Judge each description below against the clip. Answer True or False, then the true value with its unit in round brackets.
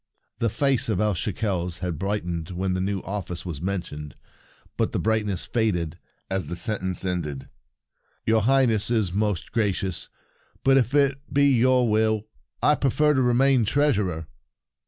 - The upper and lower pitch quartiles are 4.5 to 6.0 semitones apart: True (5.1 semitones)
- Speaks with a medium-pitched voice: False (105 Hz)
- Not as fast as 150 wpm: False (160 wpm)